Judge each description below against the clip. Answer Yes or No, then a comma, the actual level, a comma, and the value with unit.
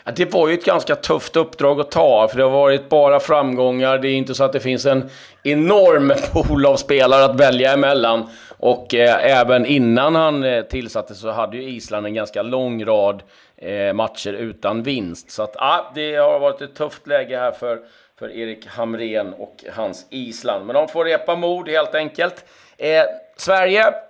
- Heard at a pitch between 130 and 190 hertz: Yes, low, 135 Hz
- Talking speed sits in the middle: Yes, average, 185 wpm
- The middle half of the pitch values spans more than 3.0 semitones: Yes, average, 4.5 semitones